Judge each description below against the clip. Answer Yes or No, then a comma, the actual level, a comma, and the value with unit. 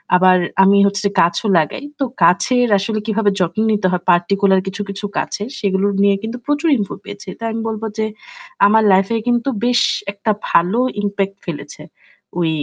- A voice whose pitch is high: Yes, high, 200 Hz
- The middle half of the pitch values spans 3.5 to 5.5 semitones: No, average, 2.9 semitones